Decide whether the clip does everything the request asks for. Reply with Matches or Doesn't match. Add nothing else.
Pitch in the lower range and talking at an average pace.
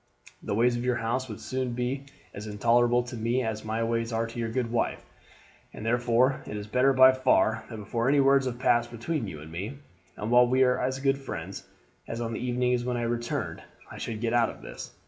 Doesn't match